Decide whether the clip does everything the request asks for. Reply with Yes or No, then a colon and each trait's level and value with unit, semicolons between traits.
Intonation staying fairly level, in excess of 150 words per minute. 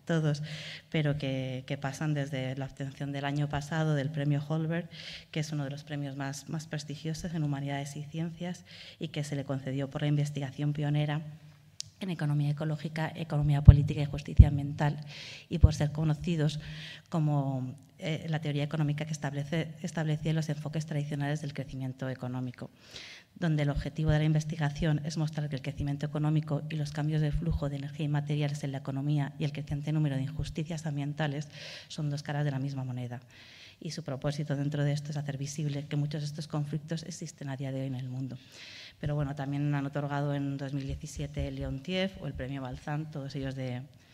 Yes: narrow, 1.7 semitones; fast, 190 wpm